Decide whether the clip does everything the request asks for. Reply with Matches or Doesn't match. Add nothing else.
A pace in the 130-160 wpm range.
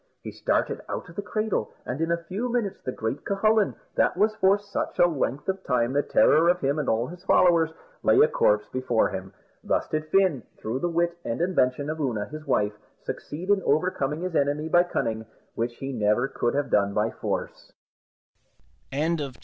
Doesn't match